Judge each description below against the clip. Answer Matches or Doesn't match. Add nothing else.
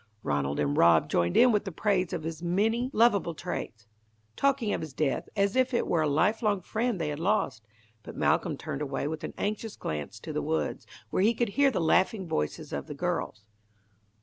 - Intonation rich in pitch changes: Matches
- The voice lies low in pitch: Doesn't match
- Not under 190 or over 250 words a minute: Matches